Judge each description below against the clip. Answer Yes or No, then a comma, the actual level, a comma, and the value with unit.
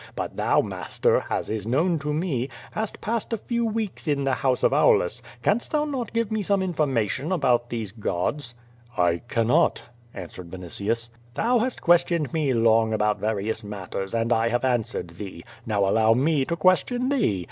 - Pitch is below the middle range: Yes, low, 130 Hz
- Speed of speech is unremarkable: Yes, average, 175 wpm